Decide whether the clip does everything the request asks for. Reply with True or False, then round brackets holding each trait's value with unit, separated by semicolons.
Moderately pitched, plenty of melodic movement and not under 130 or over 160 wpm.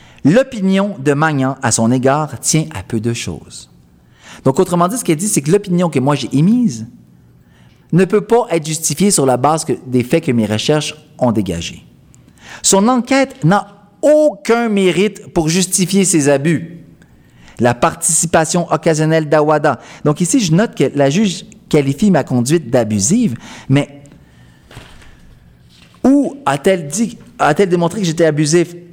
True (160 Hz; 6.6 semitones; 150 wpm)